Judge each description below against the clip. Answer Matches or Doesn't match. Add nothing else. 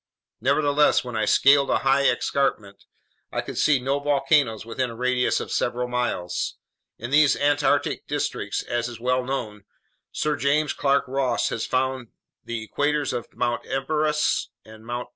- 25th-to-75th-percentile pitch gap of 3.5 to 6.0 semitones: Doesn't match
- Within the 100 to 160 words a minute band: Matches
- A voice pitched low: Matches